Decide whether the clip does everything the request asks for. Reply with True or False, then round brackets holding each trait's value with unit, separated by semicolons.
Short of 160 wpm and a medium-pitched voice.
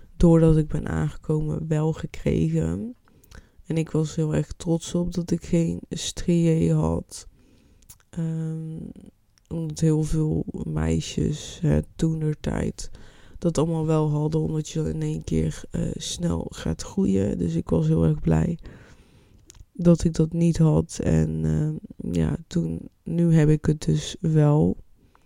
True (140 wpm; 155 Hz)